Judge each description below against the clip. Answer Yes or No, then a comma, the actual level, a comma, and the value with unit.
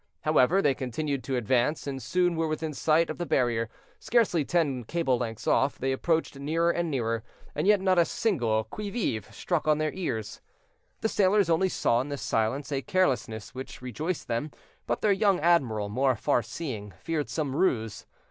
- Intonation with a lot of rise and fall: Yes, wide, 5.8 semitones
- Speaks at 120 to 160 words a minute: No, average, 185 wpm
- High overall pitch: No, medium, 145 Hz